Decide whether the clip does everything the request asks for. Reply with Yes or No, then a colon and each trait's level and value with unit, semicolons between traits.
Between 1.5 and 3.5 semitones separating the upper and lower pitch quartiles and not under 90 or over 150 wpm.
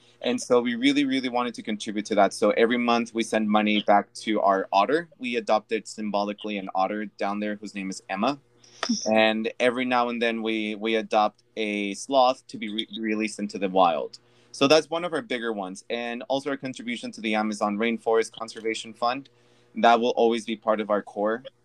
No: average, 2.8 semitones; average, 200 wpm